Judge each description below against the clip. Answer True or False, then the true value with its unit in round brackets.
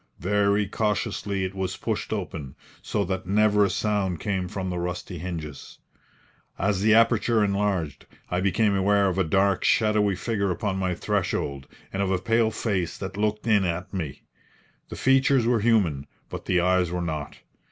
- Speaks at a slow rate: False (170 wpm)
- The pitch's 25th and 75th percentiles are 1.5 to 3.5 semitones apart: True (2.6 semitones)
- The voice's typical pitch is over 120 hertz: False (95 Hz)